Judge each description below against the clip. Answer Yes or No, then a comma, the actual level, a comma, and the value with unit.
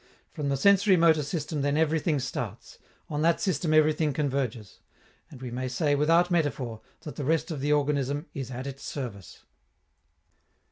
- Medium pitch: Yes, medium, 145 Hz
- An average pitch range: Yes, average, 3.0 semitones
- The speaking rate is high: No, average, 160 wpm